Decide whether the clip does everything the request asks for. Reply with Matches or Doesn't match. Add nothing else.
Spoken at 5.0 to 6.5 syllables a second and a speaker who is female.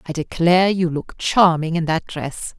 Doesn't match